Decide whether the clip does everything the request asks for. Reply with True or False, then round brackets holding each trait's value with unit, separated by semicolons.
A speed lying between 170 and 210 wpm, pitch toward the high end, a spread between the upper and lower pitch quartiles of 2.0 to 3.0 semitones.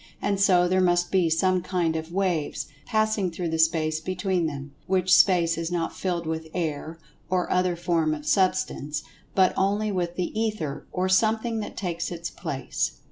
False (175 wpm; 175 Hz; 2.6 semitones)